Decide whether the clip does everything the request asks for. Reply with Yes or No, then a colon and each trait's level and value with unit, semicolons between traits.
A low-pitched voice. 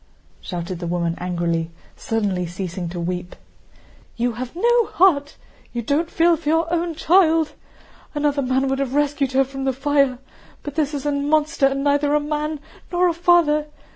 No: very high, 285 Hz